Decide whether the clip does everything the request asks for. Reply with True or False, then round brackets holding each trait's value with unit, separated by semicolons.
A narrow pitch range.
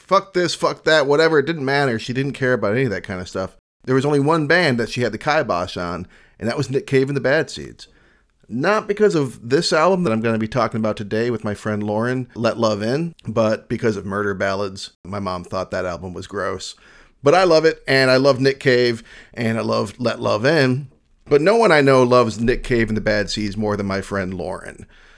False (4.8 semitones)